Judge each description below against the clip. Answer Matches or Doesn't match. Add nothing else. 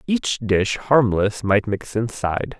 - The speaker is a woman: Doesn't match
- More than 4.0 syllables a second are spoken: Doesn't match